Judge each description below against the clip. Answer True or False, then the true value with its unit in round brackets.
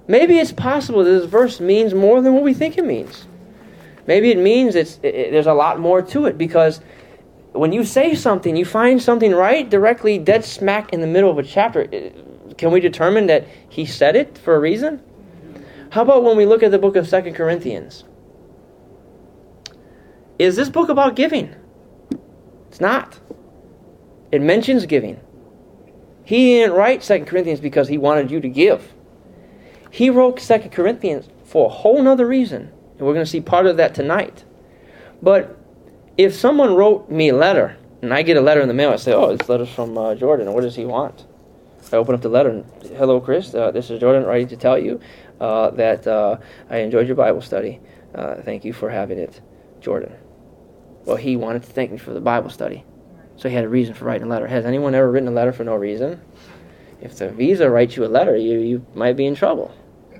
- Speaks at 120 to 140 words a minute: False (200 wpm)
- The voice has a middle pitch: True (180 Hz)